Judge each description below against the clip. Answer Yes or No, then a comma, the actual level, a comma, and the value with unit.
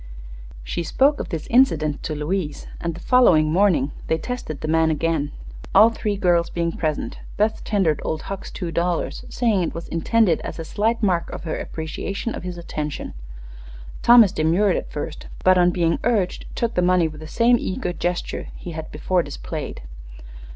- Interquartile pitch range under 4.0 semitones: No, average, 4.3 semitones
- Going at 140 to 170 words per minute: No, average, 180 wpm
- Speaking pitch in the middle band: Yes, medium, 175 Hz